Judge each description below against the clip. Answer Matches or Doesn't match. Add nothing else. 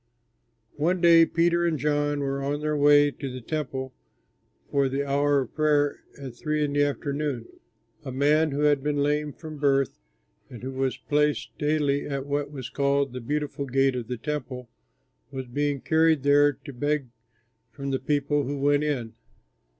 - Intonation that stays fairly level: Matches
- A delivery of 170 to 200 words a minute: Matches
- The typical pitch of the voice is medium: Matches